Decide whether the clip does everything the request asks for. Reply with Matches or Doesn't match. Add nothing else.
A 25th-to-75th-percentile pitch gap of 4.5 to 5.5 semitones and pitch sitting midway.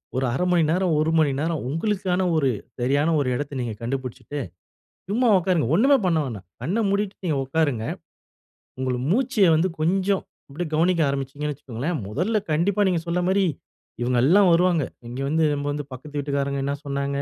Matches